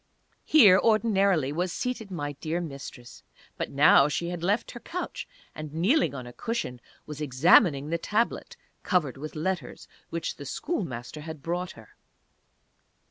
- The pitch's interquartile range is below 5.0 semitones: No, wide, 5.4 semitones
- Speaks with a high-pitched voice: No, medium, 165 Hz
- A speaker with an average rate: Yes, average, 145 wpm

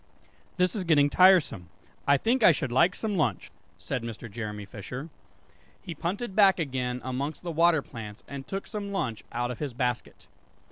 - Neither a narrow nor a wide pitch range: No, wide, 7.0 semitones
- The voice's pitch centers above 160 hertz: No, medium, 140 Hz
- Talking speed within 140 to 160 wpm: No, average, 175 wpm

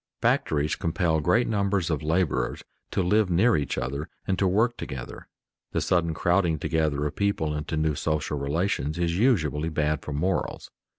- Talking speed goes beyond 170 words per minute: No, average, 165 wpm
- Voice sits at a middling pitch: No, very low, 80 Hz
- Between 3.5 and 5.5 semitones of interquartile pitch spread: Yes, average, 3.8 semitones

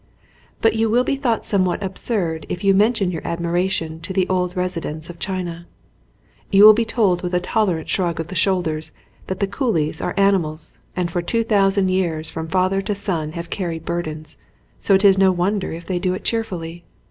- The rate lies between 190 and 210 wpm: Yes, average, 200 wpm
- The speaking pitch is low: No, medium, 185 Hz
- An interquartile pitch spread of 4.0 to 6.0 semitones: No, average, 2.9 semitones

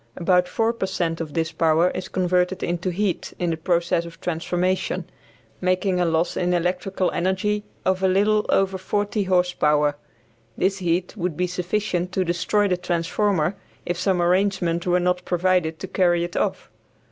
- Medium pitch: Yes, medium, 180 Hz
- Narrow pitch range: Yes, narrow, 1.6 semitones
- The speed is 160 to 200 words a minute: Yes, average, 170 wpm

